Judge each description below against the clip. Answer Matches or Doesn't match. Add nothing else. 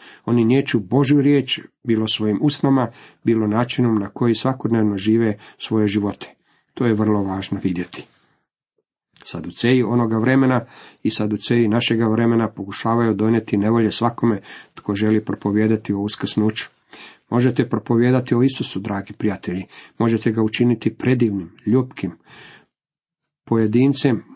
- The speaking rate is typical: Matches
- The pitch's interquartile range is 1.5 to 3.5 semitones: Matches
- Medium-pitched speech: Doesn't match